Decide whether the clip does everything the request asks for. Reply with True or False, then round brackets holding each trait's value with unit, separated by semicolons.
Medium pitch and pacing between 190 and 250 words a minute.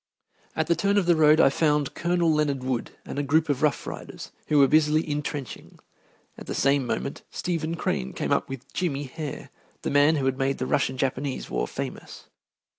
True (145 Hz; 195 wpm)